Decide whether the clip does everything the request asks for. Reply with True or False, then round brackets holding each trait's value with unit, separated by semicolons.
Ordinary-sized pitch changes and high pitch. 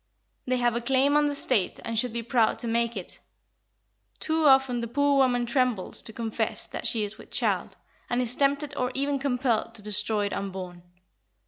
True (3.4 semitones; 245 Hz)